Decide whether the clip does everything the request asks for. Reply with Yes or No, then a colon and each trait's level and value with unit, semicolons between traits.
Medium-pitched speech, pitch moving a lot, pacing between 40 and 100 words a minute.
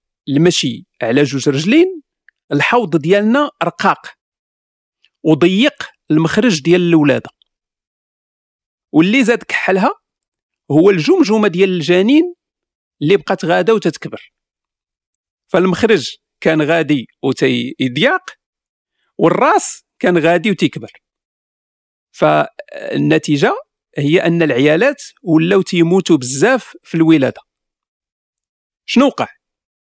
Yes: medium, 170 Hz; wide, 6.0 semitones; average, 80 wpm